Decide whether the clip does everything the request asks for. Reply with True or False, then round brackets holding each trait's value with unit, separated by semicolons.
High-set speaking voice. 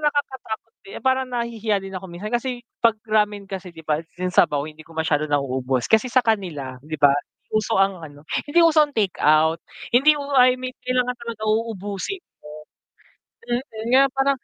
True (210 Hz)